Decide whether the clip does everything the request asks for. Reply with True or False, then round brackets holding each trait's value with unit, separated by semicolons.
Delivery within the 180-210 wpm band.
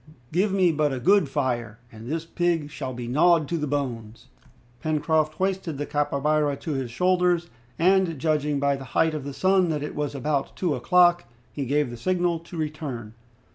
True (185 wpm)